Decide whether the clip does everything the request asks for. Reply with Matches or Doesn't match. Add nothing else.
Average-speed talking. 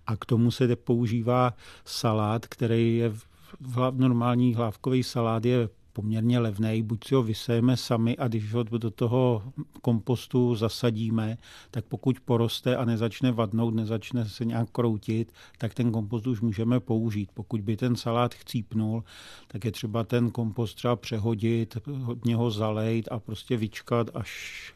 Matches